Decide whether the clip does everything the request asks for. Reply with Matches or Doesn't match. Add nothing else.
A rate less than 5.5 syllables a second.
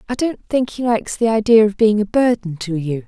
Doesn't match